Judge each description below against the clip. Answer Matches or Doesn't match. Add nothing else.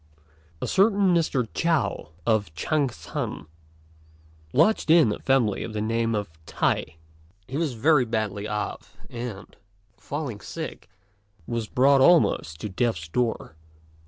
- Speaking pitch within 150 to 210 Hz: Doesn't match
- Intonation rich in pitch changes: Matches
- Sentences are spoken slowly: Matches